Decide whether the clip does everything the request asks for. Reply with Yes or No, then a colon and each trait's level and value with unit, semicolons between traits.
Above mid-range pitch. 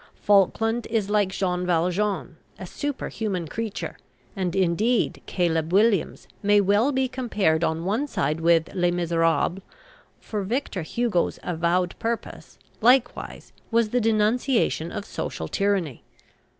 Yes: high, 195 Hz